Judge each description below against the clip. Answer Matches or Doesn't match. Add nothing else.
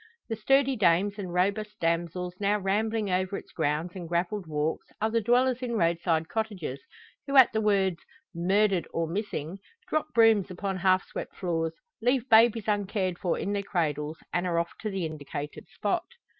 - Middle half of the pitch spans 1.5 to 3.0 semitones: Doesn't match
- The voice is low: Doesn't match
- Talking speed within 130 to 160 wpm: Doesn't match